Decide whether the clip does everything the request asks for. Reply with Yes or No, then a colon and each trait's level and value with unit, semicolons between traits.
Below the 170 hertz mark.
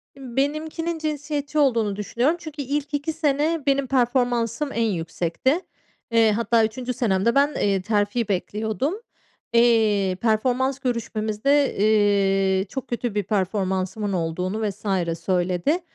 No: high, 230 Hz